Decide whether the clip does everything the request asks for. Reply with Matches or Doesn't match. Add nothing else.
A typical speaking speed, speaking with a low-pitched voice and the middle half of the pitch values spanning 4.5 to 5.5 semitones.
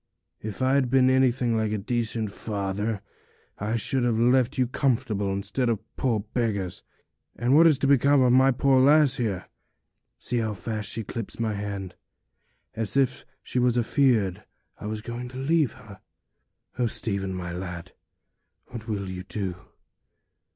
Doesn't match